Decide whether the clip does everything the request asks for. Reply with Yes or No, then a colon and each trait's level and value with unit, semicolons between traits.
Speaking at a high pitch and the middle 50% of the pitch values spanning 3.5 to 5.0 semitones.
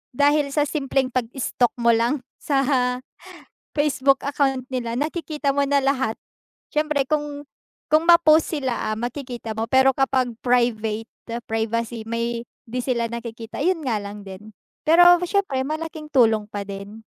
Yes: very high, 260 Hz; average, 4.1 semitones